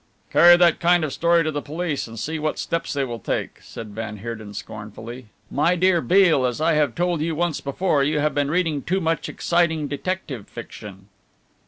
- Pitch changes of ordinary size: No, wide, 5.9 semitones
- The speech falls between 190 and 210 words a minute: Yes, average, 200 wpm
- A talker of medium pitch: Yes, medium, 150 Hz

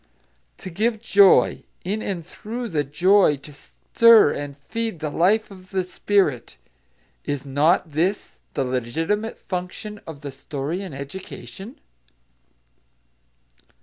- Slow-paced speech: Yes, slow, 120 wpm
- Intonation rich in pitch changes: Yes, wide, 6.1 semitones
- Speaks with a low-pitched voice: No, medium, 180 Hz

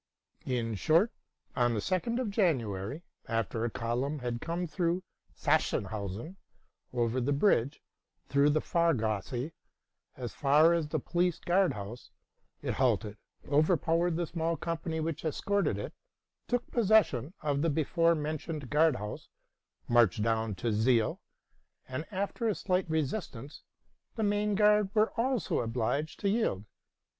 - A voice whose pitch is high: No, medium, 155 Hz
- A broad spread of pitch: Yes, wide, 6.9 semitones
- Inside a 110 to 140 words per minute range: Yes, slow, 135 wpm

